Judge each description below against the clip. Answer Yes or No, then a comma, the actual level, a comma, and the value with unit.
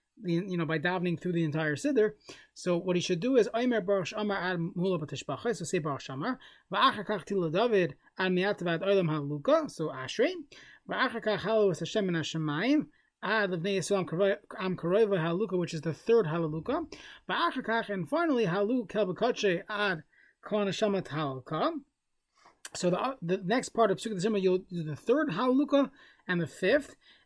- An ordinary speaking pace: Yes, average, 160 wpm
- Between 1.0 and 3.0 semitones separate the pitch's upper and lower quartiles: No, average, 4.7 semitones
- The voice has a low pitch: No, high, 195 Hz